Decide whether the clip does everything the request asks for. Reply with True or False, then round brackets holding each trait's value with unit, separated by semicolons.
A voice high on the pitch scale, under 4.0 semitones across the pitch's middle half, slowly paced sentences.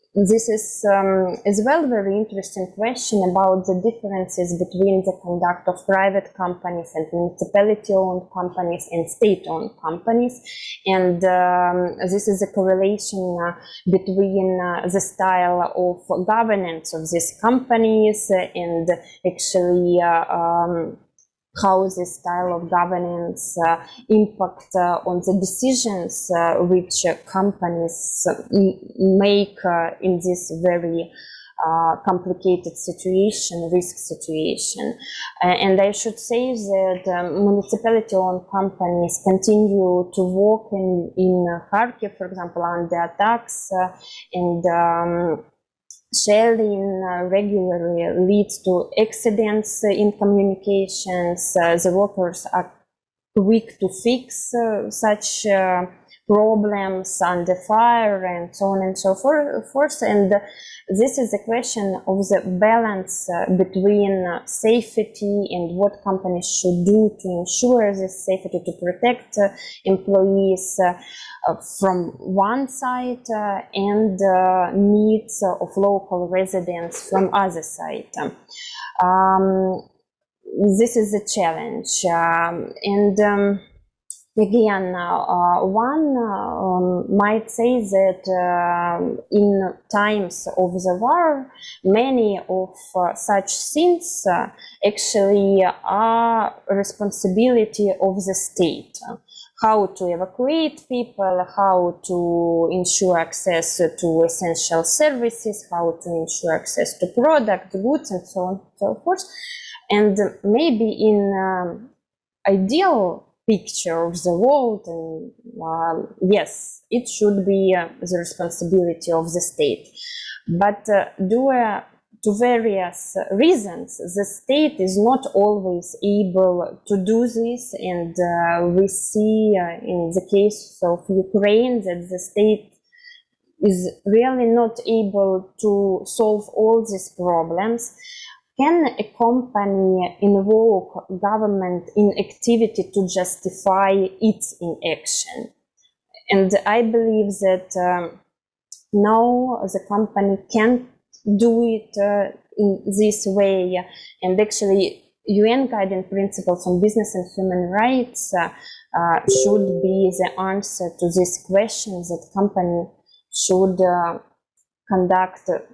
True (195 Hz; 3.0 semitones; 120 wpm)